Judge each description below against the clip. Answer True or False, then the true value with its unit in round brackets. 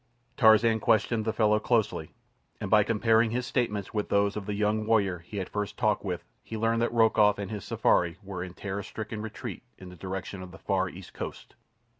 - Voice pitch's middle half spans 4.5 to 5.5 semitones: False (2.4 semitones)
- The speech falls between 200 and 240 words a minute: True (205 wpm)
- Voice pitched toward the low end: True (105 Hz)